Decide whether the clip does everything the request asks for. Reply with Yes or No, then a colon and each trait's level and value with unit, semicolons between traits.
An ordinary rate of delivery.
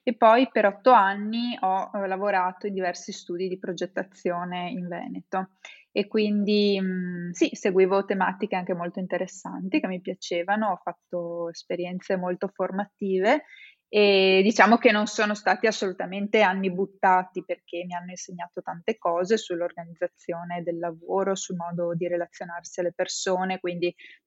Yes: average, 135 wpm